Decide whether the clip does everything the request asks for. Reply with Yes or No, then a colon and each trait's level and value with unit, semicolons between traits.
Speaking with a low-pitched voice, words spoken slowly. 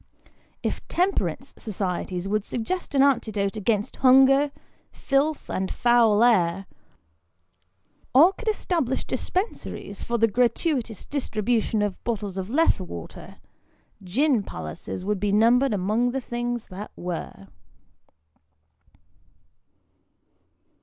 No: high, 230 Hz; slow, 105 wpm